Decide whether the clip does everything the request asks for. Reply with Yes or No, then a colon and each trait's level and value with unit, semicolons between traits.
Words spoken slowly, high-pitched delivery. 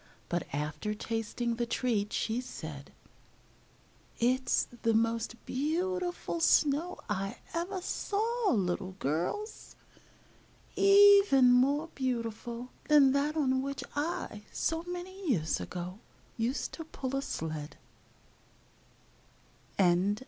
Yes: slow, 100 wpm; very high, 255 Hz